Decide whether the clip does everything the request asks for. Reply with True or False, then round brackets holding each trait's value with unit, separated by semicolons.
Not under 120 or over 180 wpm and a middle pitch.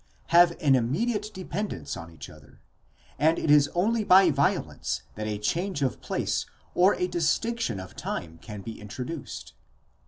True (155 wpm; 150 Hz)